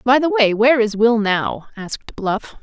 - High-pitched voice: Yes, high, 230 Hz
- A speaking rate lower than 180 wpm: No, fast, 205 wpm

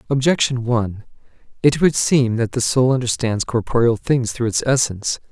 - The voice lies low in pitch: Yes, low, 120 Hz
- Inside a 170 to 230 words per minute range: No, average, 160 wpm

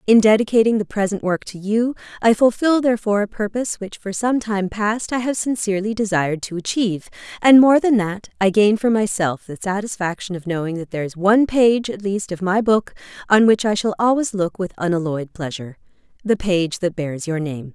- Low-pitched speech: No, high, 200 Hz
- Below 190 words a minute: No, average, 200 wpm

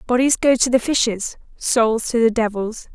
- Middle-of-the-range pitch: No, high, 235 Hz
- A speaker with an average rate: Yes, average, 185 wpm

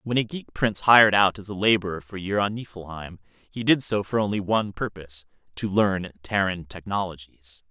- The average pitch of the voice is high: No, low, 100 Hz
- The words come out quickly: No, average, 185 wpm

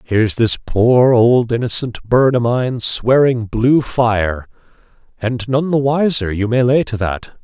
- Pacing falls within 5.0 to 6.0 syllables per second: No, 4.0 syllables/s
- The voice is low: Yes, low, 120 Hz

